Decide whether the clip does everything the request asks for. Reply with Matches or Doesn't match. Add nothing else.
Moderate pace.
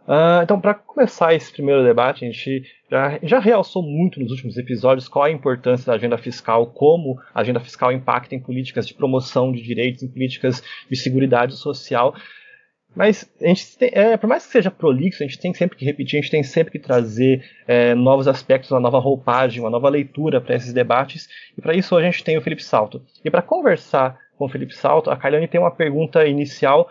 Doesn't match